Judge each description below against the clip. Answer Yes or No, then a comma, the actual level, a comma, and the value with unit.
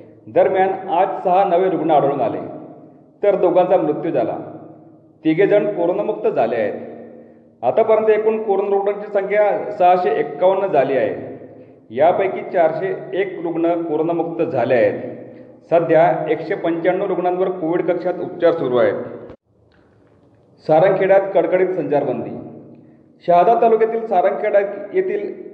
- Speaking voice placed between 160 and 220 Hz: Yes, medium, 185 Hz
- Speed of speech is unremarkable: Yes, average, 115 wpm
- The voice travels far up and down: No, average, 3.5 semitones